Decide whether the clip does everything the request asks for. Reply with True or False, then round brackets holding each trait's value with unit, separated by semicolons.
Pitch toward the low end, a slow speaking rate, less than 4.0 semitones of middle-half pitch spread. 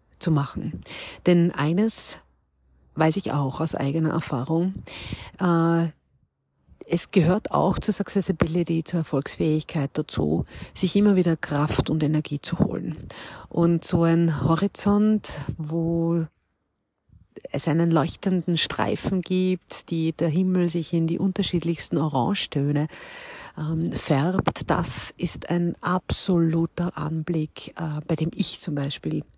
False (165 Hz; 110 wpm; 2.8 semitones)